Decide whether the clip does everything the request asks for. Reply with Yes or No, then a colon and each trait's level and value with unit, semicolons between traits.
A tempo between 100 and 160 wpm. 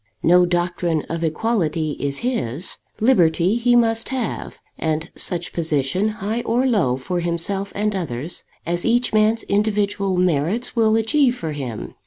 Yes: average, 145 wpm